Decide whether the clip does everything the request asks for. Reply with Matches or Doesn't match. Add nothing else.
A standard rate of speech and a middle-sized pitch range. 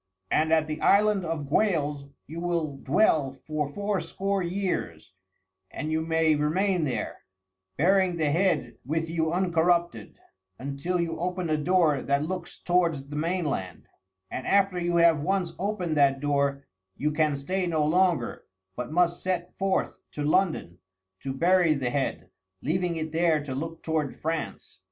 Matches